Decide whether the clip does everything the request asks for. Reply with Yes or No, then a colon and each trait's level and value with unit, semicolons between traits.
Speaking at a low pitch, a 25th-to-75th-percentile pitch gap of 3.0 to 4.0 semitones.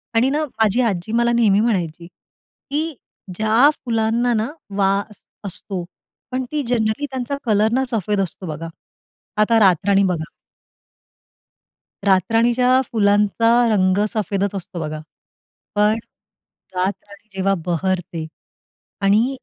No: high, 210 Hz; average, 3.7 semitones